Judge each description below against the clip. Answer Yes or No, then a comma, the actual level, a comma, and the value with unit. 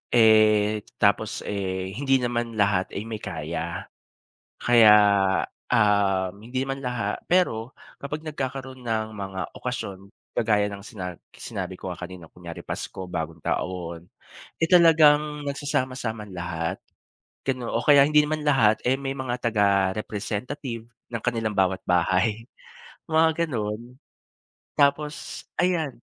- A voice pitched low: Yes, low, 115 Hz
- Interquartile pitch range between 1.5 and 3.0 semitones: No, wide, 5.4 semitones